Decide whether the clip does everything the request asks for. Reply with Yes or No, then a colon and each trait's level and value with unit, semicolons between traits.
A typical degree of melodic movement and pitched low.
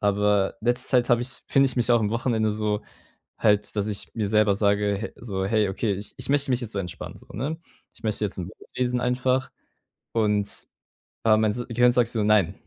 Yes: average, 3.0 semitones; low, 110 Hz